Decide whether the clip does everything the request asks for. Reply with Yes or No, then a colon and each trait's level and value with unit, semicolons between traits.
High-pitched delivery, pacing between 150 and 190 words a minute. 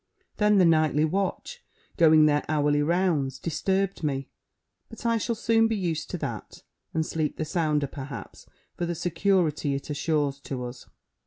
No: medium, 160 Hz; average, 160 wpm